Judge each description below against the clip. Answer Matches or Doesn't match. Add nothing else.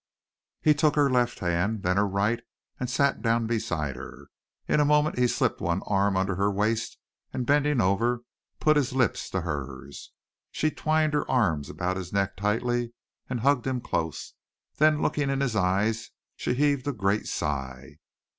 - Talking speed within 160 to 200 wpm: Matches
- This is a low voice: Matches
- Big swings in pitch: Matches